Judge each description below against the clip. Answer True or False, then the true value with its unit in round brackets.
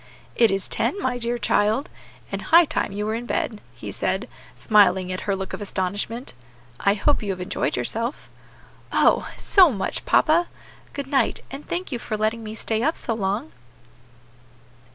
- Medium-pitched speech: False (225 Hz)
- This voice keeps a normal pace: True (175 wpm)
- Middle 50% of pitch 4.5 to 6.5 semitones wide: True (5.0 semitones)